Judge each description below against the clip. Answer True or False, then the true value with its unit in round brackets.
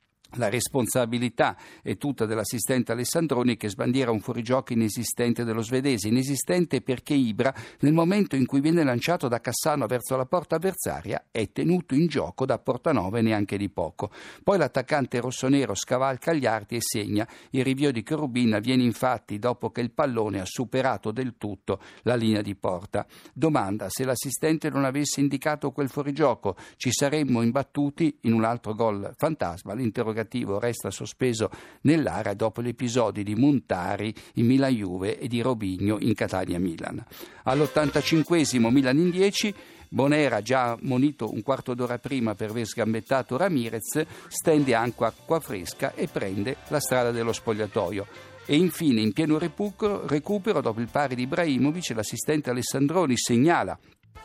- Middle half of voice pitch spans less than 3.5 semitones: False (4.0 semitones)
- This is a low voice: True (125 Hz)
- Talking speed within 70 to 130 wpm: False (145 wpm)